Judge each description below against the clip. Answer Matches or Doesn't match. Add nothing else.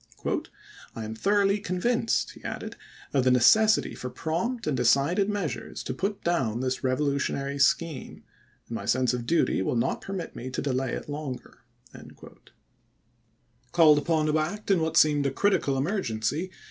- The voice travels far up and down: Matches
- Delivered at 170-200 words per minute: Doesn't match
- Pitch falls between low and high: Matches